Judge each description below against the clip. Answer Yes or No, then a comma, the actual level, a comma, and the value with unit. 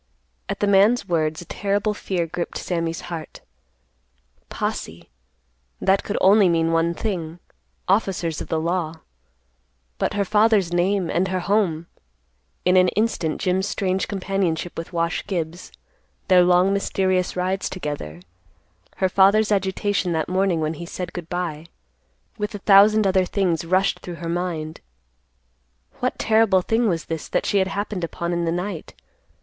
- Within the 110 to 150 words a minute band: Yes, average, 145 wpm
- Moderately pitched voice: Yes, medium, 180 Hz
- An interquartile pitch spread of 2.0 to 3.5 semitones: Yes, average, 2.9 semitones